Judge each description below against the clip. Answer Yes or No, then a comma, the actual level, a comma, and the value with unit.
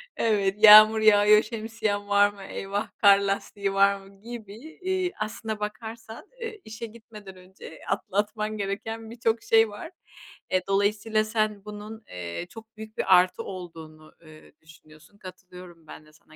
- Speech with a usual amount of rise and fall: No, narrow, 2.3 semitones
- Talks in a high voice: Yes, high, 205 Hz